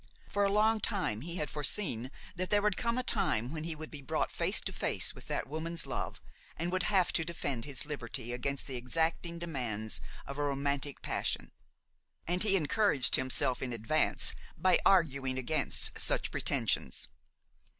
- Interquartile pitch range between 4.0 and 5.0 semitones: No, wide, 5.6 semitones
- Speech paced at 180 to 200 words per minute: No, average, 170 wpm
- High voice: No, medium, 155 Hz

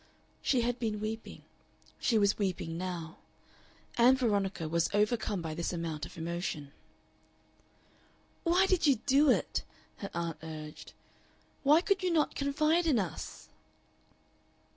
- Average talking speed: No, slow, 130 wpm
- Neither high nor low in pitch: No, high, 210 Hz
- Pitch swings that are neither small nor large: No, wide, 8.7 semitones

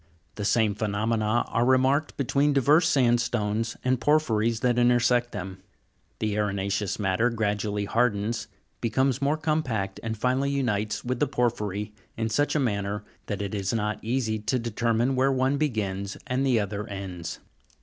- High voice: No, low, 115 Hz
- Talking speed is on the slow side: No, average, 155 wpm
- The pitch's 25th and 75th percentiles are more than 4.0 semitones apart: No, average, 3.7 semitones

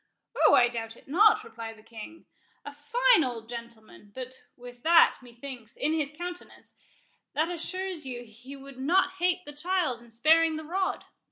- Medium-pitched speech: No, very high, 285 Hz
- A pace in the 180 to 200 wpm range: No, average, 165 wpm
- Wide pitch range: Yes, wide, 6.2 semitones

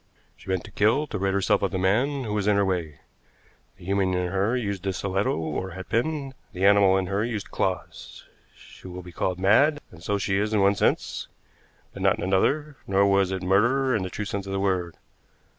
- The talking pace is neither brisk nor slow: No, fast, 220 wpm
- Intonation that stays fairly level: Yes, narrow, 2.1 semitones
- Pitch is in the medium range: No, low, 100 Hz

